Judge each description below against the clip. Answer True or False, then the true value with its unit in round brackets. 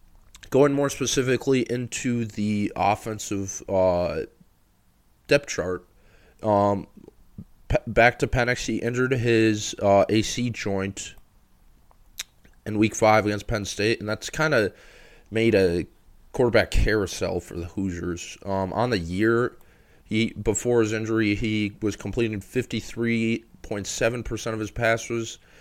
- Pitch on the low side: True (110 Hz)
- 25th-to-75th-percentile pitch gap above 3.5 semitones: False (2.7 semitones)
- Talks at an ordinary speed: False (120 wpm)